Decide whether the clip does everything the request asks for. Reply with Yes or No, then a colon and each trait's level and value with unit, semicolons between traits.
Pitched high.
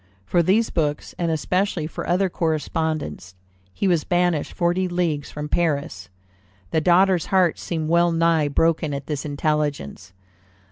No: medium, 160 Hz